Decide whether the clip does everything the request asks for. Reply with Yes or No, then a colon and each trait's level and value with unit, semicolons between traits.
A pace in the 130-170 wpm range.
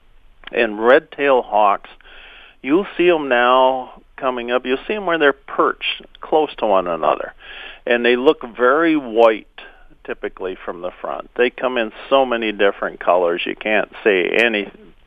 Yes: average, 160 wpm